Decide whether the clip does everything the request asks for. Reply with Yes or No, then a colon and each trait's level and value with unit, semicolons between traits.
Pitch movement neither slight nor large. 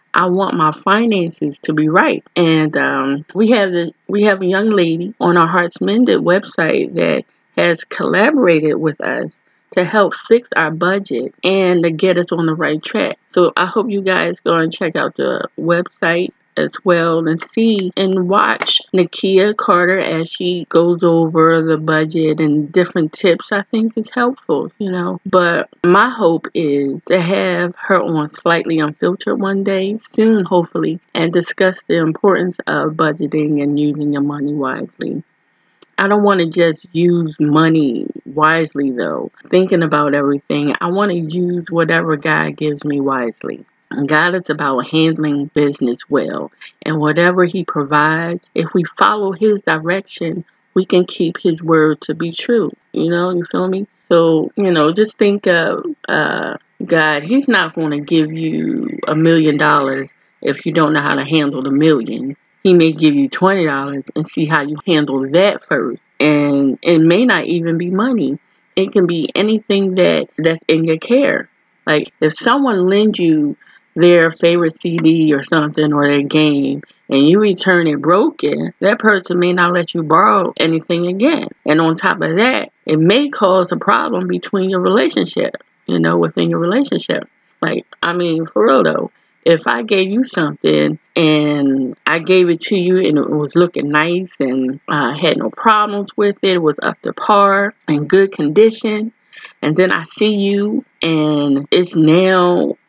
Yes: average, 3.7 semitones